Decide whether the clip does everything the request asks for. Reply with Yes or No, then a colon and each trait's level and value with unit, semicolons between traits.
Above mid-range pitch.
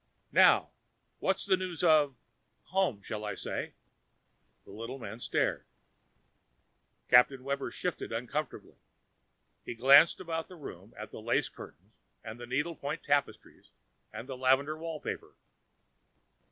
No: medium, 140 Hz